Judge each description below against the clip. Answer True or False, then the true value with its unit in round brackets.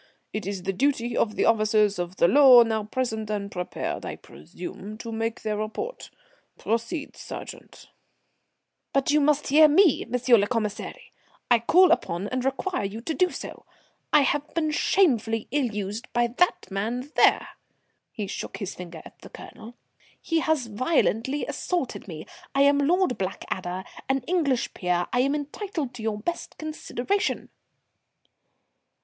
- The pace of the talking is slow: False (155 wpm)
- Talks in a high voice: True (240 Hz)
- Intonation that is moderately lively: False (5.8 semitones)